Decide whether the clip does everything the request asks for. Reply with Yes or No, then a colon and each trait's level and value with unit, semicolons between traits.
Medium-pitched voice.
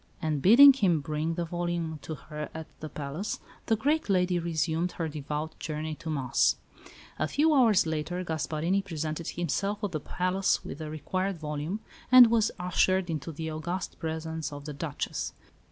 Yes: medium, 165 Hz